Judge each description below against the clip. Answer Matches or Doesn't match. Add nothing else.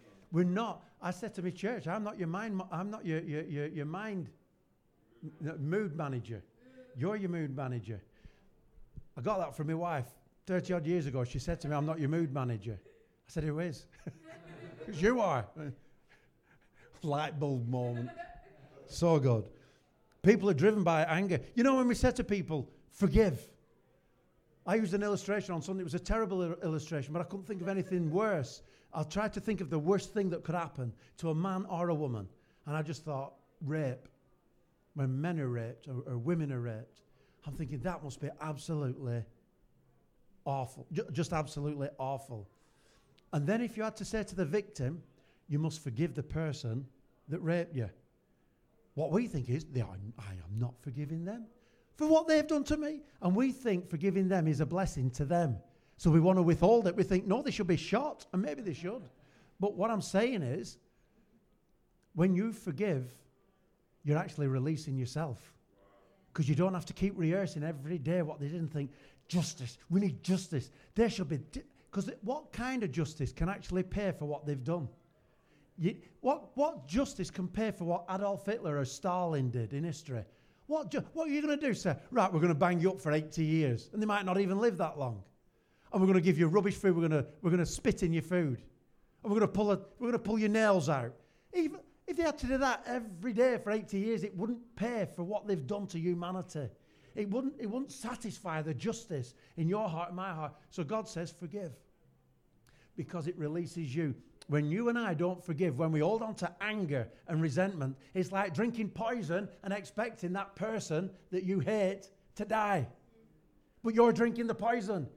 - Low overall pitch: Doesn't match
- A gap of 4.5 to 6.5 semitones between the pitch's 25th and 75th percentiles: Matches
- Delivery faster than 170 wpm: Matches